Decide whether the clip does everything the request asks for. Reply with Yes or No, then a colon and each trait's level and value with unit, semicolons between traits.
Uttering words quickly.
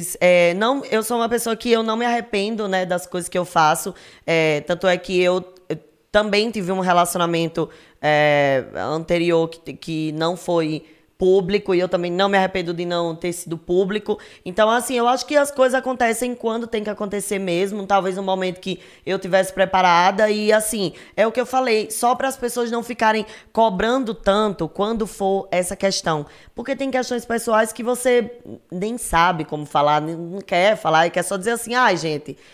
Yes: fast, 190 wpm